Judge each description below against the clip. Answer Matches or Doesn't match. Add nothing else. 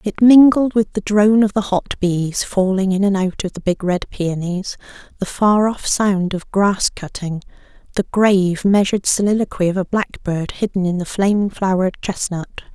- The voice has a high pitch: Matches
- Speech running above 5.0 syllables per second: Doesn't match